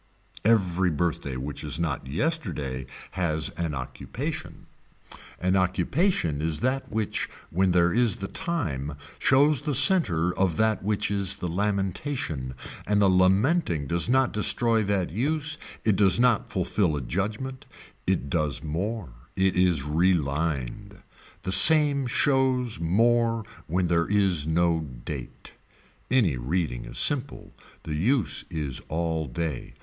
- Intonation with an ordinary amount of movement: No, wide, 6.5 semitones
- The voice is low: Yes, very low, 95 Hz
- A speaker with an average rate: No, slow, 130 wpm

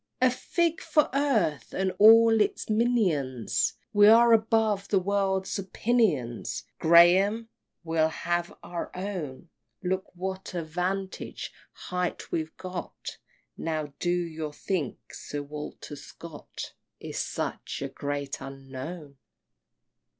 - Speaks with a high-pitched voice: No, medium, 180 Hz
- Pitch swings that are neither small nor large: Yes, average, 5.0 semitones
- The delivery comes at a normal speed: No, slow, 115 wpm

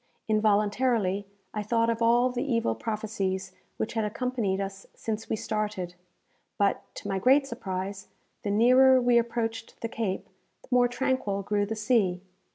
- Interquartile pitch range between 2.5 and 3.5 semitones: Yes, average, 3.1 semitones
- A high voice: Yes, high, 220 Hz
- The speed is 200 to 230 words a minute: No, average, 155 wpm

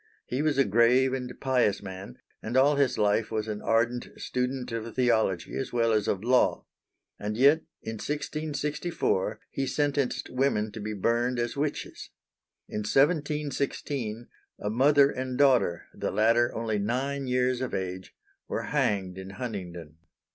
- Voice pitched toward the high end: No, low, 120 Hz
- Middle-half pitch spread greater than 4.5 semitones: No, average, 4.2 semitones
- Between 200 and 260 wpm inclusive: No, average, 150 wpm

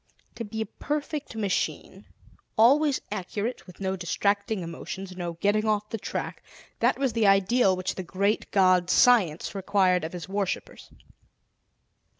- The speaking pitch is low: No, high, 200 Hz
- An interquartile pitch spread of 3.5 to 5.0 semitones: No, average, 3.1 semitones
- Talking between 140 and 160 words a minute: Yes, average, 145 wpm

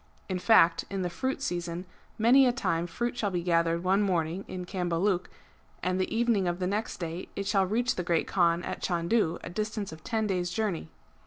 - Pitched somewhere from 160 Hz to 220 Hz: Yes, medium, 185 Hz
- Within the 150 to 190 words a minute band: No, average, 200 wpm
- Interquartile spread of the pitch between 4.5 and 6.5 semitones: No, average, 3.7 semitones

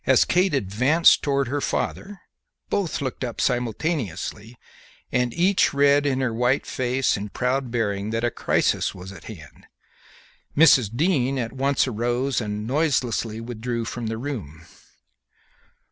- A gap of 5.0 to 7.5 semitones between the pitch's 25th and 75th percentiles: No, average, 3.8 semitones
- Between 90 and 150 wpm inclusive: Yes, average, 140 wpm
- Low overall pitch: Yes, low, 125 Hz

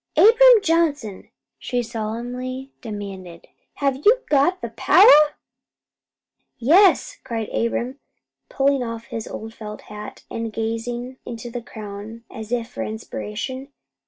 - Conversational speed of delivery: No, slow, 120 wpm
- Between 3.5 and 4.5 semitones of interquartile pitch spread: Yes, average, 3.9 semitones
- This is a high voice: Yes, high, 240 Hz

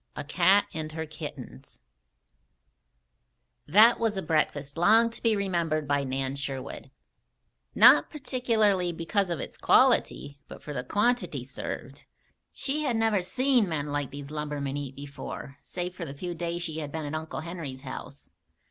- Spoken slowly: No, average, 155 wpm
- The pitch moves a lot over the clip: Yes, wide, 5.8 semitones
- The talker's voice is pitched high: No, medium, 160 Hz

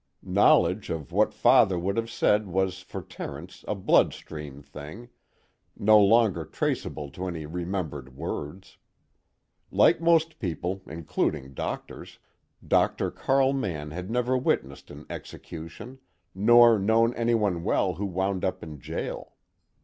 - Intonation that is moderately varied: No, wide, 6.0 semitones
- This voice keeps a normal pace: No, slow, 125 wpm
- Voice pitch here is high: No, very low, 95 Hz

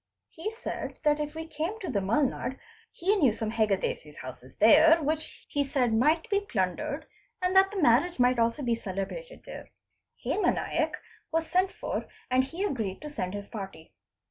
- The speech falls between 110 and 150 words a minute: No, average, 175 wpm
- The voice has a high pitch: Yes, very high, 280 Hz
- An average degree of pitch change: No, wide, 7.2 semitones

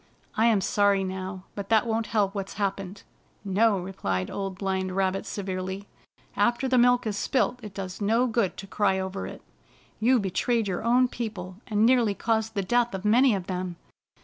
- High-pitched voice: Yes, high, 200 Hz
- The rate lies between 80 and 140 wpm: No, average, 180 wpm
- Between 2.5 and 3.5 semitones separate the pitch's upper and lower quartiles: Yes, average, 3.1 semitones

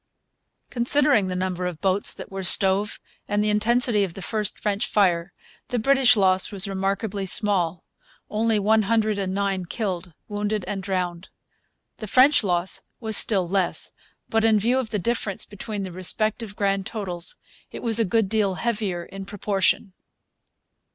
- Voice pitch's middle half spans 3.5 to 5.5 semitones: No, narrow, 2.6 semitones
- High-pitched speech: Yes, high, 200 Hz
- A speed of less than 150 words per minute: No, average, 160 wpm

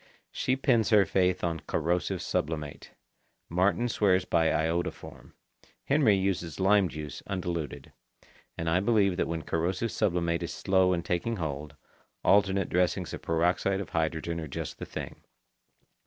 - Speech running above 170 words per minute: No, average, 140 wpm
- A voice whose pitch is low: Yes, very low, 90 Hz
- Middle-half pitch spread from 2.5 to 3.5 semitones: Yes, average, 3.0 semitones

